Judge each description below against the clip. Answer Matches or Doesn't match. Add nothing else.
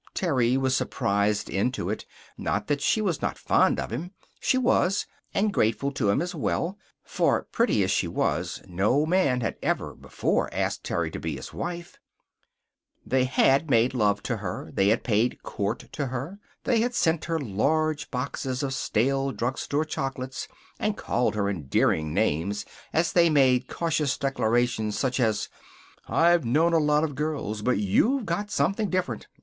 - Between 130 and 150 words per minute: Doesn't match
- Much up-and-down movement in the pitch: Matches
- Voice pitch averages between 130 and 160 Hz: Matches